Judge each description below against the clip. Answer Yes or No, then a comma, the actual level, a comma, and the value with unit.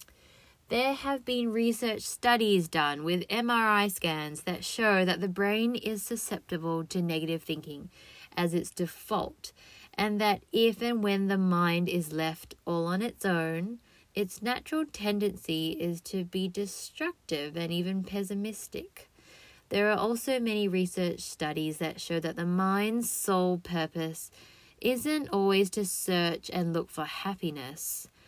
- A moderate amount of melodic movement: Yes, average, 4.1 semitones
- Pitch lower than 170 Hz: No, high, 190 Hz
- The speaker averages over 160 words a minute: No, average, 140 wpm